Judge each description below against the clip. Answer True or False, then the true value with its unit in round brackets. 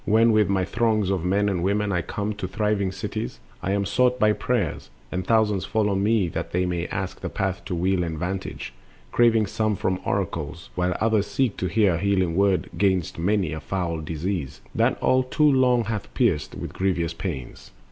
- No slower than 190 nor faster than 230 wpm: True (195 wpm)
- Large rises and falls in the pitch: False (3.1 semitones)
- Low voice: True (95 Hz)